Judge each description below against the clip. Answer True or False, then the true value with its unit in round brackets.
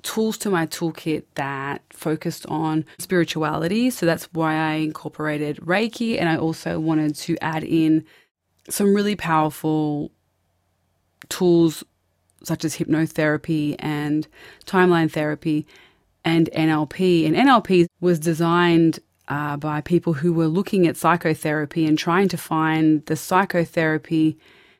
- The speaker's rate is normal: False (125 wpm)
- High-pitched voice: False (160 Hz)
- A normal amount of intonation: False (1.9 semitones)